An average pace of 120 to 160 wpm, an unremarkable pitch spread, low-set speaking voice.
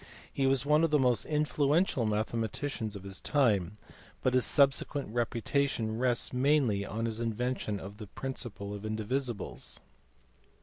Yes: average, 140 wpm; average, 4.3 semitones; low, 120 Hz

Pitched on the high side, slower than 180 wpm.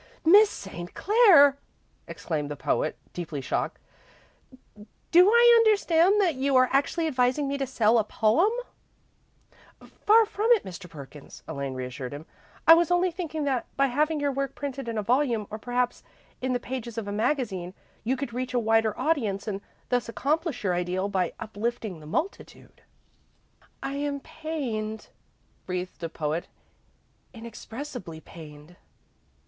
Yes: high, 245 Hz; average, 150 wpm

